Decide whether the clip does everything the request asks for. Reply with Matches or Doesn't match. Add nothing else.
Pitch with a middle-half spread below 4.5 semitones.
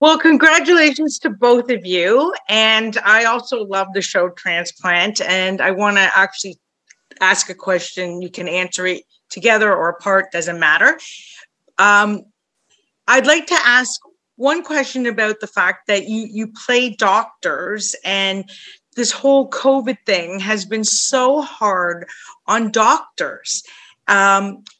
Doesn't match